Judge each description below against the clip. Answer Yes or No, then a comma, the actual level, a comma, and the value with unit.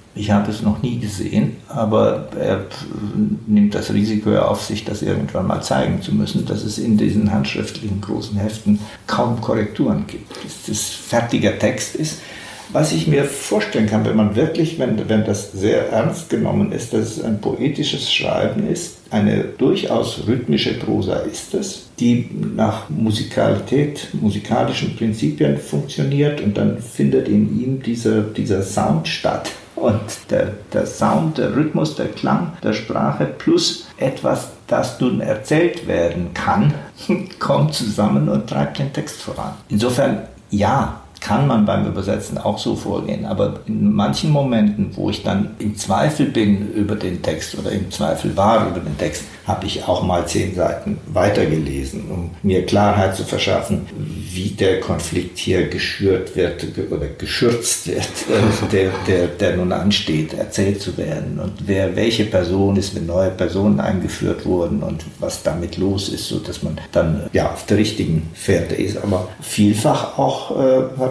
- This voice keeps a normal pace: Yes, average, 155 wpm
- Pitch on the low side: Yes, low, 105 Hz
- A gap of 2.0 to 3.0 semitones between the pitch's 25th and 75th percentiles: Yes, average, 2.7 semitones